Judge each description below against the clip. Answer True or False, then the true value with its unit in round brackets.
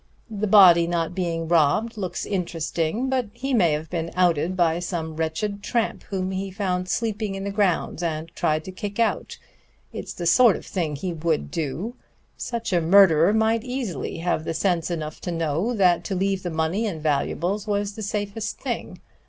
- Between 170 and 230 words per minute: True (180 wpm)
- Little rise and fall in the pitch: False (3.9 semitones)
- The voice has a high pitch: False (180 Hz)